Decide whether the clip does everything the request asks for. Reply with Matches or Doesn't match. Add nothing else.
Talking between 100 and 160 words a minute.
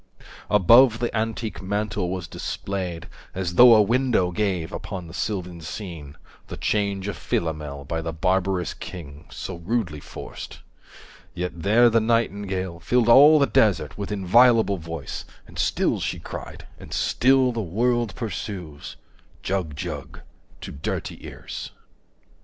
Matches